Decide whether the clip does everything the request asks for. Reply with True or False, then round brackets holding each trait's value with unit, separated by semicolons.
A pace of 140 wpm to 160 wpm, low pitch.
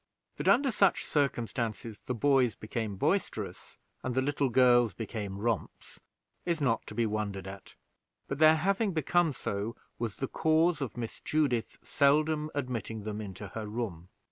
True (155 wpm; 120 Hz)